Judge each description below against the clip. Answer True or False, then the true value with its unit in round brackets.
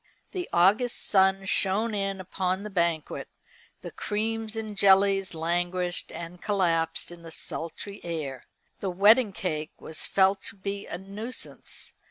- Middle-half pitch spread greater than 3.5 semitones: False (2.9 semitones)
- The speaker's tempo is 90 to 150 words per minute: True (140 wpm)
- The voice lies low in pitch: False (190 Hz)